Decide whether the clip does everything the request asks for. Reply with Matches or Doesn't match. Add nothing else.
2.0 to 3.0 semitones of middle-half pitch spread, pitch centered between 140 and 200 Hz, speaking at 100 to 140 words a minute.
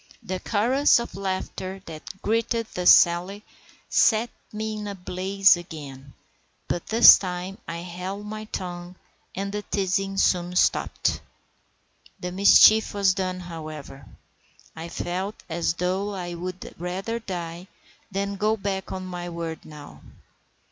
Matches